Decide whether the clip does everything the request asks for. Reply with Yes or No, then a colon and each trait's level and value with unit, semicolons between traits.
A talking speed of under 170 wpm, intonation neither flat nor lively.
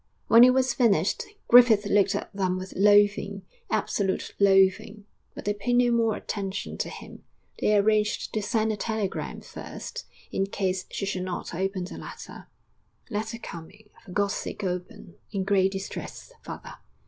No: average, 160 wpm; narrow, 2.1 semitones